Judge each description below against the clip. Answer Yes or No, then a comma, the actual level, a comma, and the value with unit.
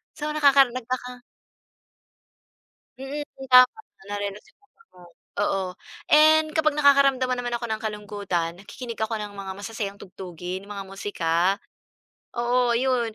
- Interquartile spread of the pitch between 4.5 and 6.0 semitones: Yes, average, 5.1 semitones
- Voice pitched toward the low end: No, high, 235 Hz